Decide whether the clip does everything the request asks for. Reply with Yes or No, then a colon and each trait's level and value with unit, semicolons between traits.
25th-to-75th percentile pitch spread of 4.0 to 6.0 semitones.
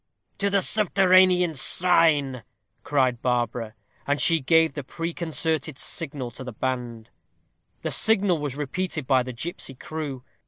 Yes: average, 5.1 semitones